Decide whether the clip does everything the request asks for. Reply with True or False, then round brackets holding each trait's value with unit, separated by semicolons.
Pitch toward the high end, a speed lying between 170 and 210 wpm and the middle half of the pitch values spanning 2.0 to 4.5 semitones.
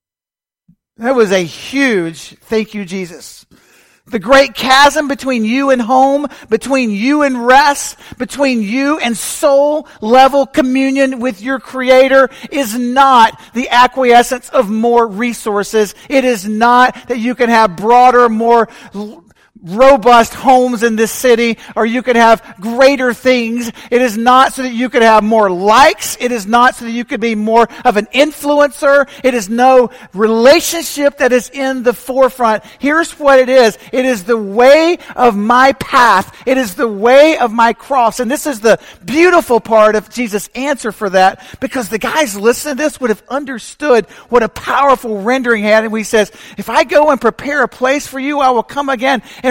True (245 Hz; 175 wpm; 3.1 semitones)